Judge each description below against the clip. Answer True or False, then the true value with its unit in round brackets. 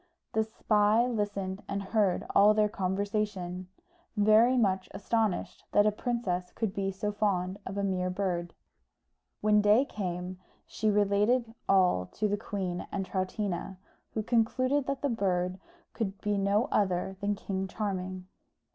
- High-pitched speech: True (200 Hz)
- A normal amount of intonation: False (2.3 semitones)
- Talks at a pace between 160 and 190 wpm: False (145 wpm)